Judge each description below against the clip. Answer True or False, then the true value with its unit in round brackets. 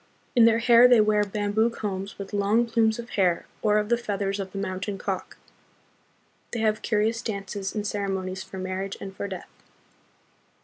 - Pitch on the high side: True (205 Hz)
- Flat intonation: True (2.3 semitones)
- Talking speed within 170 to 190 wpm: True (175 wpm)